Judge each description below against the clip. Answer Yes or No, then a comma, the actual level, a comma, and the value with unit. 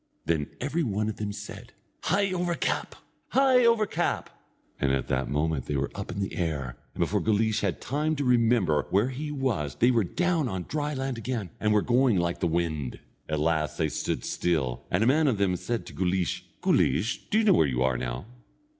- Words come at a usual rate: No, fast, 210 wpm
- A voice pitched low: Yes, low, 100 Hz